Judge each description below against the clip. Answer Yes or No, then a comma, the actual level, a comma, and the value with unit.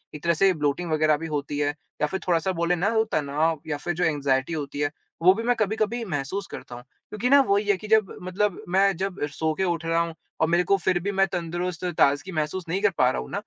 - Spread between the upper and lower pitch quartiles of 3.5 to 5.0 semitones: Yes, average, 4.2 semitones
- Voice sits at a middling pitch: Yes, medium, 170 Hz